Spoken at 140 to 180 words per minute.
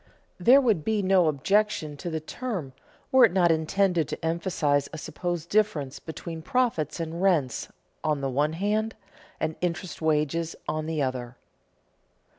Yes: average, 150 wpm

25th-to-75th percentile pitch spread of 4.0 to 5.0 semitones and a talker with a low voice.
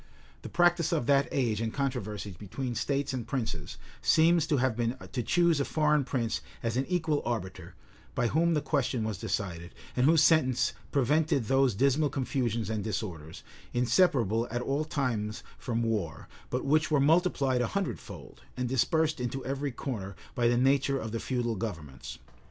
Yes: average, 4.4 semitones; low, 125 Hz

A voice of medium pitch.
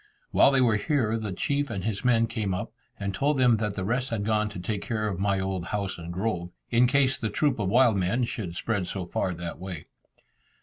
No: low, 105 Hz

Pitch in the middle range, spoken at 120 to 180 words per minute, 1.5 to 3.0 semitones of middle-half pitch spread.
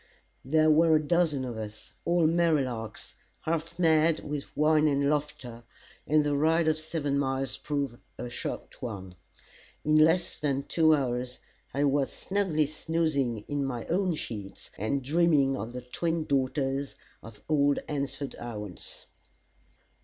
No: medium, 145 Hz; average, 145 wpm; average, 3.4 semitones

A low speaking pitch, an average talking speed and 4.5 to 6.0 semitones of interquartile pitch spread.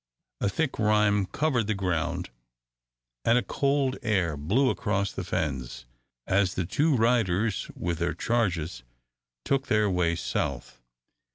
No: low, 100 Hz; slow, 130 wpm; average, 5.2 semitones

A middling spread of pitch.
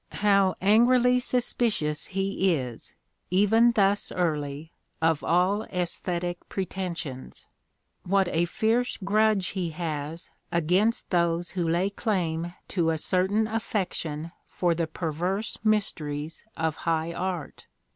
Yes: average, 3.8 semitones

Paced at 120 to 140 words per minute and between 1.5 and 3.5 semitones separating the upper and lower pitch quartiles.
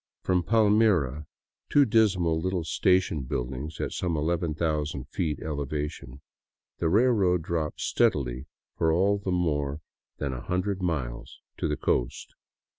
No: slow, 135 wpm; average, 4.2 semitones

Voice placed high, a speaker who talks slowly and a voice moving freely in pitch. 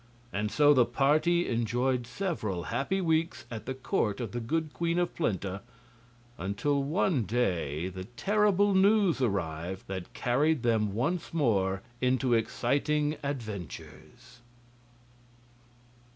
No: low, 125 Hz; slow, 120 wpm; wide, 7.3 semitones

